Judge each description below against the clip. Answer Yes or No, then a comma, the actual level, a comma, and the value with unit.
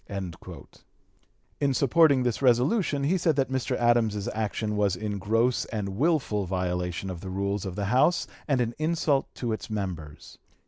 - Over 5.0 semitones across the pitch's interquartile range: Yes, wide, 5.5 semitones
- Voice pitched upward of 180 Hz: No, low, 110 Hz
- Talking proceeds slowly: No, average, 155 wpm